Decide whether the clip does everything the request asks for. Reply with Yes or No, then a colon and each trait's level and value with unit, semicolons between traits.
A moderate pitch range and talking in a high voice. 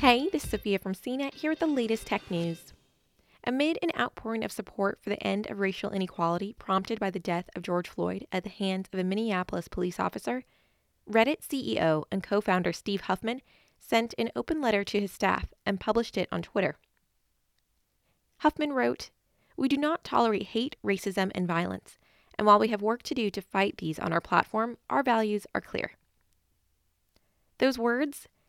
Yes: average, 4.4 semitones; high, 200 Hz